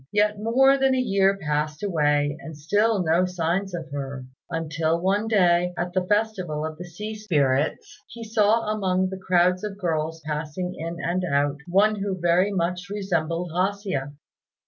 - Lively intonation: No, average, 4.2 semitones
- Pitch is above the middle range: No, medium, 180 Hz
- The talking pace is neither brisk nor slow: Yes, average, 170 wpm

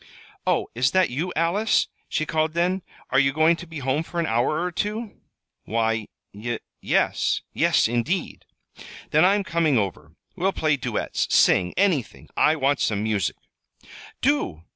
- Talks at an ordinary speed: Yes, average, 155 wpm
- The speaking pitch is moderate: Yes, medium, 155 Hz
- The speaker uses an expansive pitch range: Yes, wide, 6.9 semitones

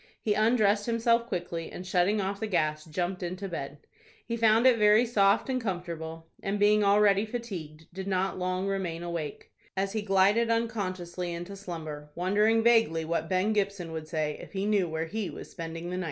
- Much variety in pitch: No, average, 3.8 semitones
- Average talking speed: Yes, average, 185 wpm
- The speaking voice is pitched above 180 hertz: Yes, high, 190 Hz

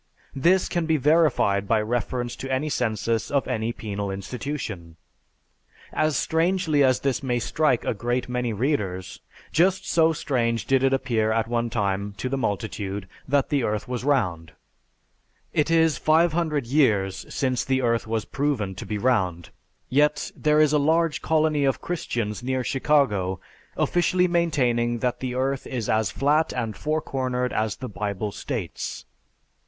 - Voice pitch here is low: Yes, low, 125 Hz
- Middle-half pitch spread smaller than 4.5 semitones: No, average, 5.3 semitones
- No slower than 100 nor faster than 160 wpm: Yes, average, 155 wpm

